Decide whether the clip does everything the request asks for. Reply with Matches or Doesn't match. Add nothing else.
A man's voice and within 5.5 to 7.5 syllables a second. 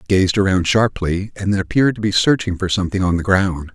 Matches